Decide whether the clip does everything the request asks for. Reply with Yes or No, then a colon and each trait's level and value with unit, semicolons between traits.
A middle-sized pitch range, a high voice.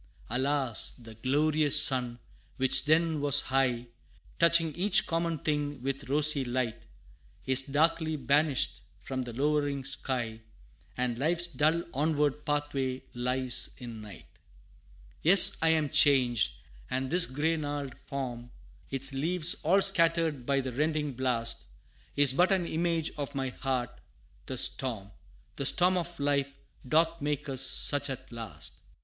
No: average, 3.4 semitones; medium, 140 Hz